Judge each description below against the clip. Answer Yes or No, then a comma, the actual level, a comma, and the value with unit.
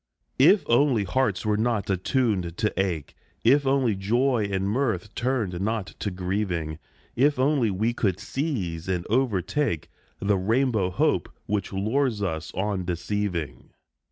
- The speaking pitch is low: Yes, low, 105 Hz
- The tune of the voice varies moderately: Yes, average, 4.9 semitones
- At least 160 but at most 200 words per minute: No, slow, 135 wpm